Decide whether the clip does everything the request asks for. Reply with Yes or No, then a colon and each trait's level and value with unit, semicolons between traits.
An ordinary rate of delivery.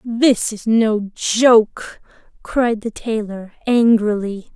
No: slow, 105 wpm